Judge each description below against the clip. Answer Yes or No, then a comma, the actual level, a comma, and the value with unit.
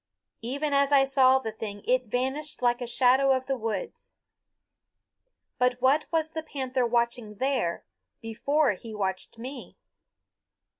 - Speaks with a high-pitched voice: Yes, very high, 255 Hz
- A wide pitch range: No, average, 3.2 semitones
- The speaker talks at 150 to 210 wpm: No, average, 140 wpm